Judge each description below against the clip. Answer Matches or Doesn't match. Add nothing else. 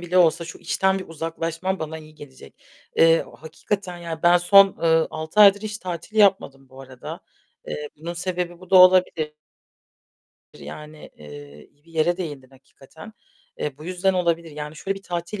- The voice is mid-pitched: Matches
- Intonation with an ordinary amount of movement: Matches